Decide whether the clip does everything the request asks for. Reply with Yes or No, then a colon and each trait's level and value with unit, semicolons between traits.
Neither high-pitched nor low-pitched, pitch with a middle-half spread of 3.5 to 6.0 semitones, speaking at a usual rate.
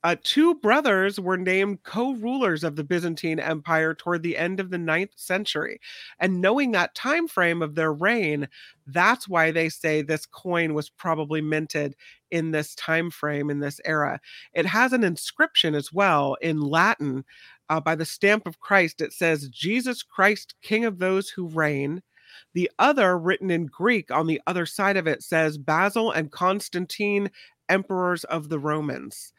Yes: medium, 170 Hz; average, 3.9 semitones; average, 170 wpm